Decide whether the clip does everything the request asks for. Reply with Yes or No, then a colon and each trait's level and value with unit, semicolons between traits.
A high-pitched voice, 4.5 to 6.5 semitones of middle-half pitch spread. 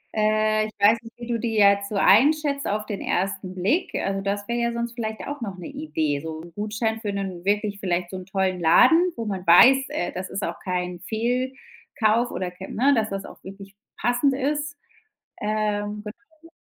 No: high, 215 Hz; average, 3.8 semitones